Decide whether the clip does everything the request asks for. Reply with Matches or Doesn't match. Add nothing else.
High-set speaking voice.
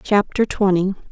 Matches